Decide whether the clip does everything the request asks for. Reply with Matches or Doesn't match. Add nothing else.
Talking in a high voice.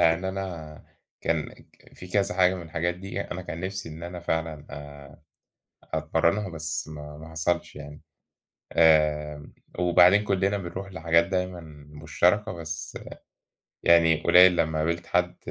Doesn't match